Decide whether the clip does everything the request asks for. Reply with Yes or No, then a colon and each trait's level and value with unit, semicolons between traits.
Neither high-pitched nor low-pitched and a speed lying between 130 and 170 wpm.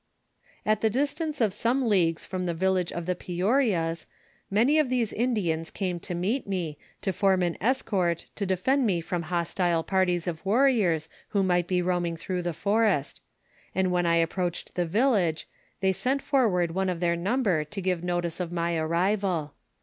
No: medium, 180 Hz; average, 180 wpm